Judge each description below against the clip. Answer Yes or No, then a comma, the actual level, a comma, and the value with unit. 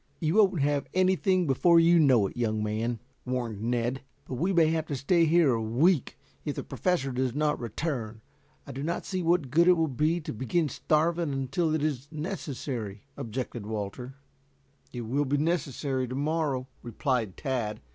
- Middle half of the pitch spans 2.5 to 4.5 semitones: No, average, 5.2 semitones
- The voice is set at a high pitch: No, medium, 140 Hz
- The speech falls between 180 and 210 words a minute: Yes, average, 185 wpm